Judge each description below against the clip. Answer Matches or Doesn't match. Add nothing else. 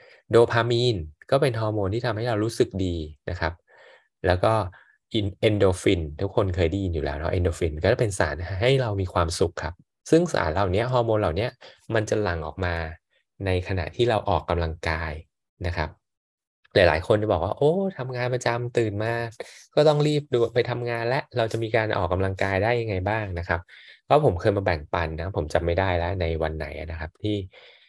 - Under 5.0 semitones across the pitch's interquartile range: Doesn't match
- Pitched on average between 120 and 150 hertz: Doesn't match